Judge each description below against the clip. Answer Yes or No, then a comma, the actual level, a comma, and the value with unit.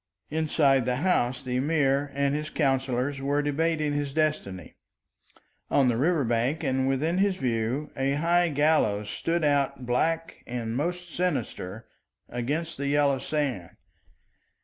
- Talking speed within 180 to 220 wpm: No, slow, 135 wpm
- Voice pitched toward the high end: No, medium, 140 Hz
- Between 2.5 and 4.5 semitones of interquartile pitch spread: Yes, average, 3.6 semitones